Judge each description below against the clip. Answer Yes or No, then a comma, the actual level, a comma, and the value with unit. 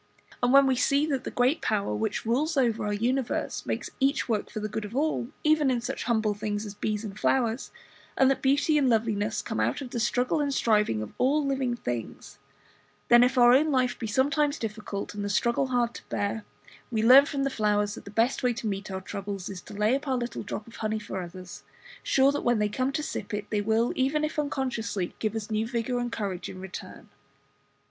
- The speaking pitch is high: Yes, high, 235 Hz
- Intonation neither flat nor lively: Yes, average, 4.2 semitones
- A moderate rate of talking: No, fast, 225 wpm